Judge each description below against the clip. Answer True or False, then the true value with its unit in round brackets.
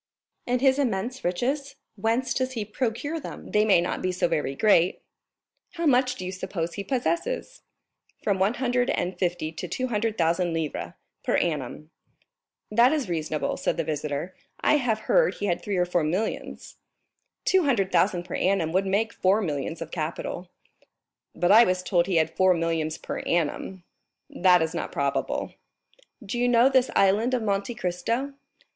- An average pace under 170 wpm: False (175 wpm)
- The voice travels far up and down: True (6.0 semitones)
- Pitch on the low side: False (195 Hz)